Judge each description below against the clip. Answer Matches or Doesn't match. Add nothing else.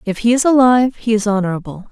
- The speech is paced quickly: Matches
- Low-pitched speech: Doesn't match